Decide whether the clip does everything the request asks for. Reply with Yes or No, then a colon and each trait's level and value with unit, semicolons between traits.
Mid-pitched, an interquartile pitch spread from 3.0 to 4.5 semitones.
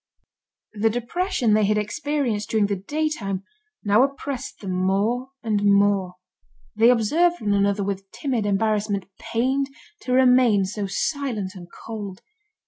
No: high, 215 Hz; average, 4.1 semitones